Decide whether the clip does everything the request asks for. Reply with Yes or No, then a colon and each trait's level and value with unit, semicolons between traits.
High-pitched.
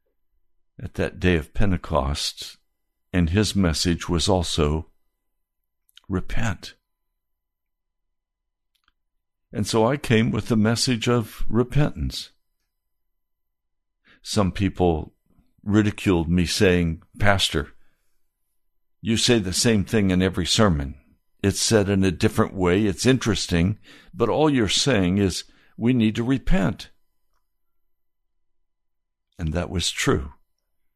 No: very low, 90 Hz